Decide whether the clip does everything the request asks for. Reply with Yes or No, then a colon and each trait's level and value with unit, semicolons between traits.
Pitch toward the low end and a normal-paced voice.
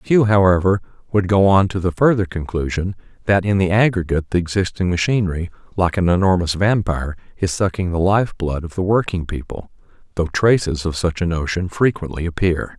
Yes: very low, 90 Hz; average, 170 wpm